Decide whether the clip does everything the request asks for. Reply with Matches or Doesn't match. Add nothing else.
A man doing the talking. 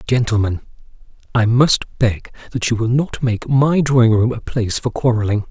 Matches